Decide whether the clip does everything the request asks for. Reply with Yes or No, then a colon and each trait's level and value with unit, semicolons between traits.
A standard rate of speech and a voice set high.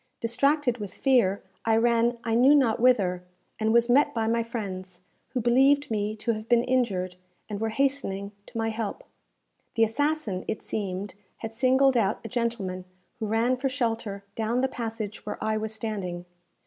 Yes: average, 175 wpm; high, 225 Hz